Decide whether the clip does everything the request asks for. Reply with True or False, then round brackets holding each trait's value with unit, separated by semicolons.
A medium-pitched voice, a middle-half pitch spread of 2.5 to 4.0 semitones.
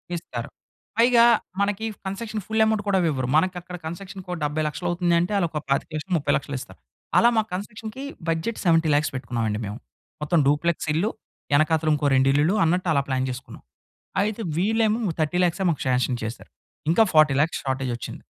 False (165 Hz; 5.3 semitones)